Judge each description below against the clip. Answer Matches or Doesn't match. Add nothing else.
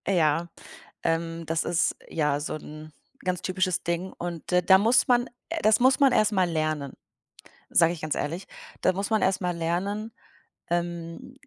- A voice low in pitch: Doesn't match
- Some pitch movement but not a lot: Matches